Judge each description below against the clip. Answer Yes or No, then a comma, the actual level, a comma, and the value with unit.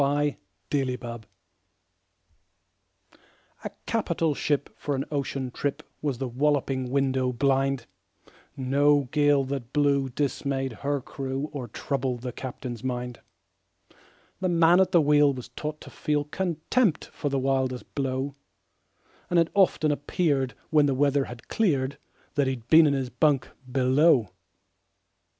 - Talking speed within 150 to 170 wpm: No, average, 140 wpm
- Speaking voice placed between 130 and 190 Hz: Yes, medium, 140 Hz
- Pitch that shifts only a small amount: Yes, narrow, 2.1 semitones